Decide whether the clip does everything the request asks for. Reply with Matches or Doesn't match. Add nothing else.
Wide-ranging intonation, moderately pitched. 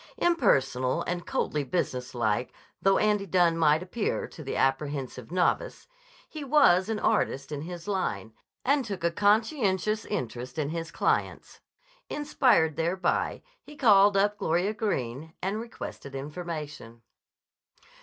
Matches